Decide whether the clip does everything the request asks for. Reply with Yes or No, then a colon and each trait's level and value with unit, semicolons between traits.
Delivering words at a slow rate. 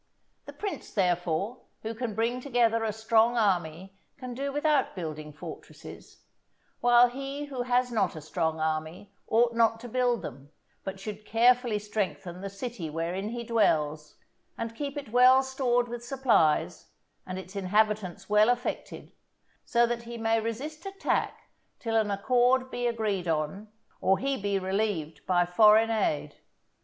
No: average, 150 wpm